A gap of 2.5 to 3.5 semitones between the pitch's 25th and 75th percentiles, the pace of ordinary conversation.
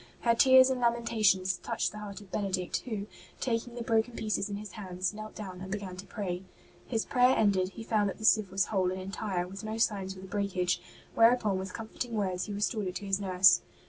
No: average, 2.9 semitones; fast, 220 wpm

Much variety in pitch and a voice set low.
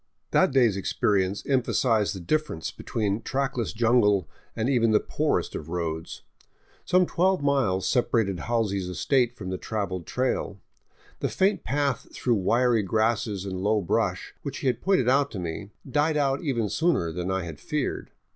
Yes: wide, 5.9 semitones; low, 115 Hz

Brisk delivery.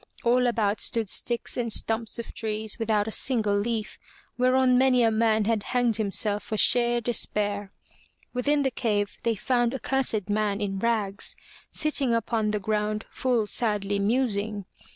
No: average, 155 wpm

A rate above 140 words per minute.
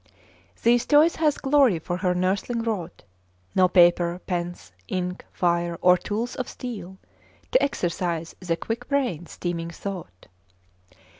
No: slow, 135 wpm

